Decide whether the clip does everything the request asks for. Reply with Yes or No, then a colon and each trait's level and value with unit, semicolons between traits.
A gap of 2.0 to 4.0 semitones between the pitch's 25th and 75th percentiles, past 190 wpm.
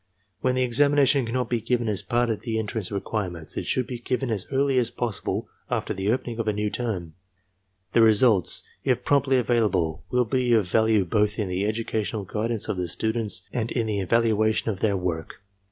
Yes: average, 3.1 semitones; average, 200 wpm